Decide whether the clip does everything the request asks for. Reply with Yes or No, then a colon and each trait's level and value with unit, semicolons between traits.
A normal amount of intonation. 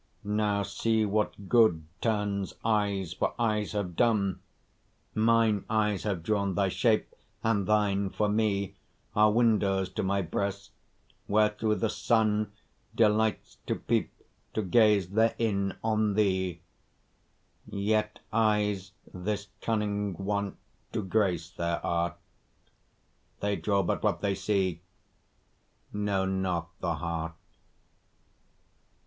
No: narrow, 2.0 semitones